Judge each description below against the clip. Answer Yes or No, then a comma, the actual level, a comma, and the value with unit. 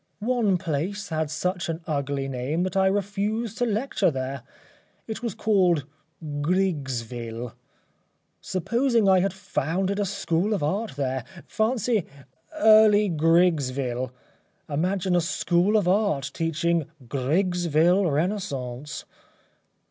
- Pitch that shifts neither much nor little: No, wide, 5.7 semitones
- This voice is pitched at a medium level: Yes, medium, 175 Hz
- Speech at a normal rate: No, slow, 110 wpm